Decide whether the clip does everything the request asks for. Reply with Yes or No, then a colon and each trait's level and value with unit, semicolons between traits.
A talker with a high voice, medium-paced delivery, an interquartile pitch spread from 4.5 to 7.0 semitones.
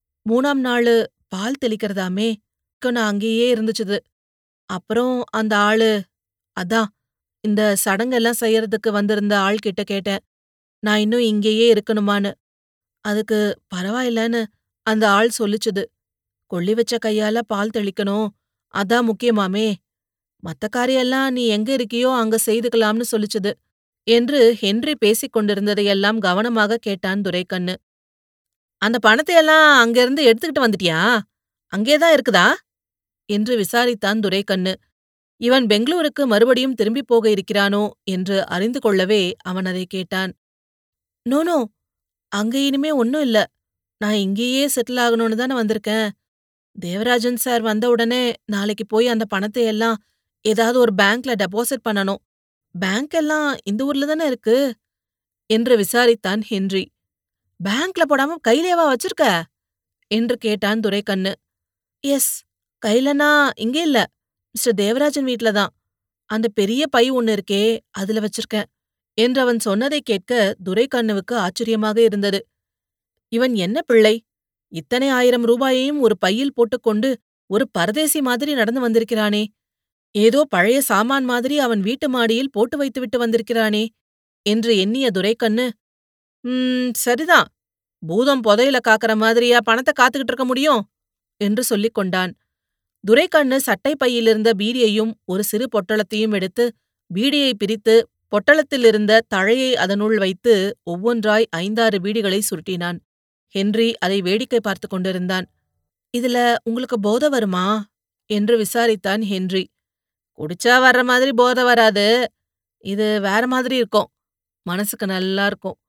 No: high, 220 Hz; average, 110 wpm; average, 3.2 semitones